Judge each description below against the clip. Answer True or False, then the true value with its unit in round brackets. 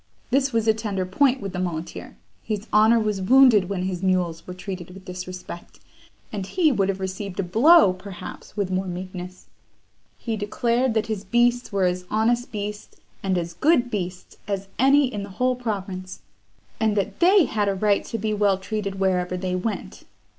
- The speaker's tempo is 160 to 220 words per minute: True (180 wpm)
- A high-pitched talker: True (200 Hz)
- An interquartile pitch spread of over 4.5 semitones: False (3.5 semitones)